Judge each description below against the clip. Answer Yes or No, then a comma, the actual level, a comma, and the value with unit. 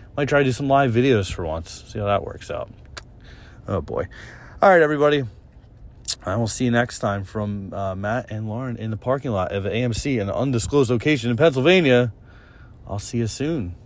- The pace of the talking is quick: No, average, 195 wpm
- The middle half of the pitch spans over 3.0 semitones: Yes, average, 4.5 semitones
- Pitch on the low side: Yes, low, 115 Hz